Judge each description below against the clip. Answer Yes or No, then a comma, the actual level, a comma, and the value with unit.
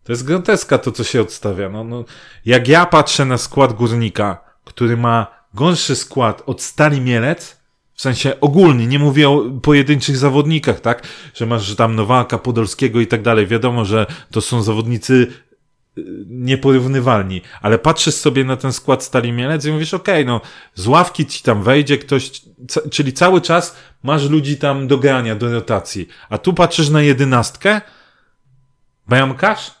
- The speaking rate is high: Yes, fast, 165 wpm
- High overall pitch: No, low, 130 Hz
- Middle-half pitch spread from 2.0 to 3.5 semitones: No, average, 4.2 semitones